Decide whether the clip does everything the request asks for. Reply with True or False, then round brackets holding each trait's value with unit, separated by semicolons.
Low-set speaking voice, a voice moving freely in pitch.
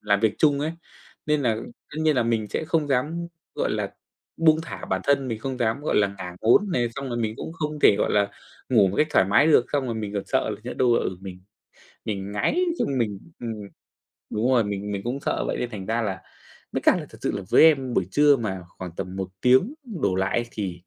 True (115 Hz; 5.8 semitones)